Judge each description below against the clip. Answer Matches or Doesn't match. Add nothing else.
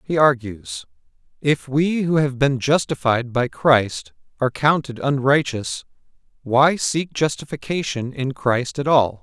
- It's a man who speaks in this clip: Matches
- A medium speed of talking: Doesn't match